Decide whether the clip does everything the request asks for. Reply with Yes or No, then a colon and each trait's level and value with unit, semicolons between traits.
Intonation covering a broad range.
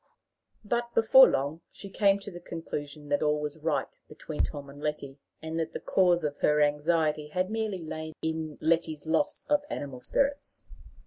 No: average, 4.0 semitones